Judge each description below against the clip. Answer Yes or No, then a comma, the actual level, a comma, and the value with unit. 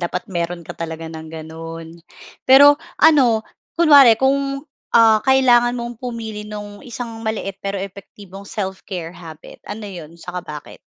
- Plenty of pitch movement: Yes, wide, 6.0 semitones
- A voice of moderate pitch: No, high, 205 Hz